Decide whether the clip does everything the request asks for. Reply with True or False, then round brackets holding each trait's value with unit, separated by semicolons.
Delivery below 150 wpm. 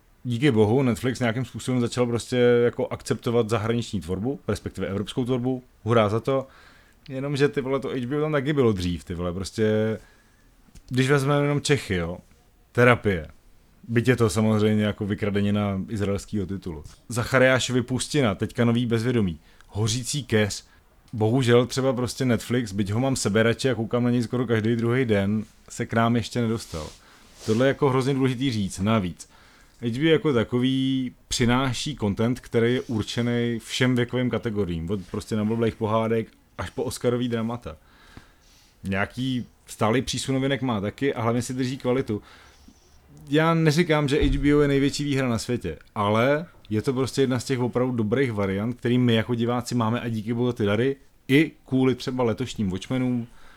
False (160 wpm)